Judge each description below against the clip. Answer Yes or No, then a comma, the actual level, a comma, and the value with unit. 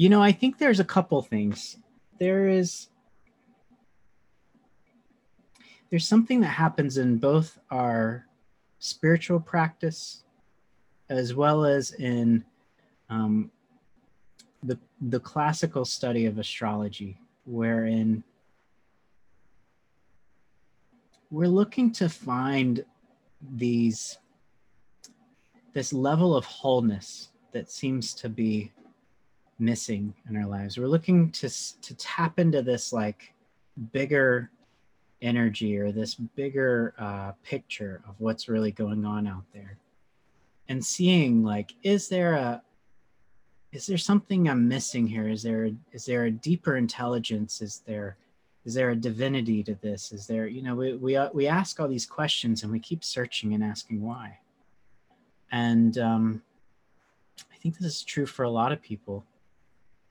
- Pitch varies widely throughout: Yes, wide, 6.0 semitones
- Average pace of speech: No, slow, 125 wpm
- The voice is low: Yes, low, 125 Hz